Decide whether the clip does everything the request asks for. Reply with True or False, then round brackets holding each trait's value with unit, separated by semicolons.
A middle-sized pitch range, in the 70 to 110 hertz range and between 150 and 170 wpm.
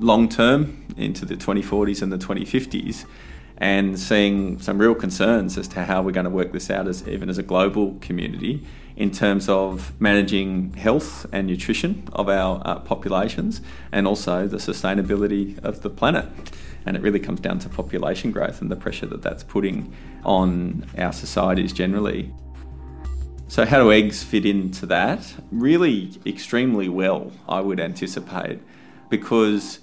False (2.2 semitones; 95 Hz; 155 wpm)